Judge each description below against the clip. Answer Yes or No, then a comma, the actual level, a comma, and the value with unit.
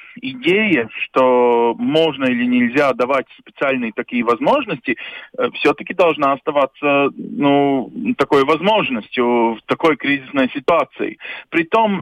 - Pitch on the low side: No, medium, 145 Hz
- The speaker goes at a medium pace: No, slow, 105 wpm